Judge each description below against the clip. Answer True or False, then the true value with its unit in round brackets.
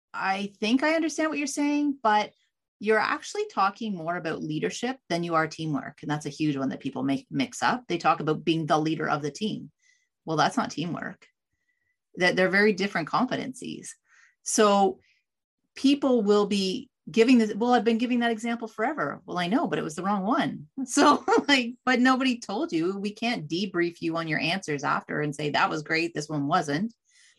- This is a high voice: True (215 Hz)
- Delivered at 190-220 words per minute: True (195 wpm)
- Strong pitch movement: True (7.8 semitones)